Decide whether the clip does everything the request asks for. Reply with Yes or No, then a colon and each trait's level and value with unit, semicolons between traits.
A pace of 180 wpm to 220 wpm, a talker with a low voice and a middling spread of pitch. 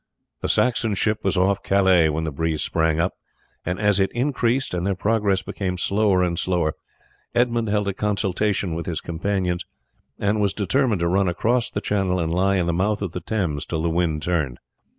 Yes: average, 200 wpm; very low, 95 Hz; average, 3.3 semitones